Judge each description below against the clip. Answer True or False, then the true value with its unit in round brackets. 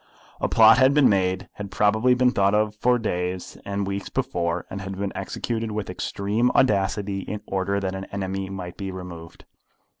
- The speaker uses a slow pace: False (180 wpm)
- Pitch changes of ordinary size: False (2.1 semitones)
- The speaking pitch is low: True (100 Hz)